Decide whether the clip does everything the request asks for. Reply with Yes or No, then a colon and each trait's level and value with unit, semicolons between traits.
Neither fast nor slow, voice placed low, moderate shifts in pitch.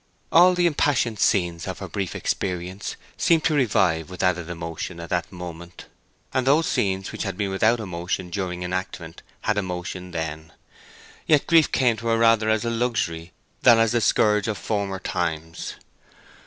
Yes: average, 170 wpm; very low, 95 Hz; average, 4.8 semitones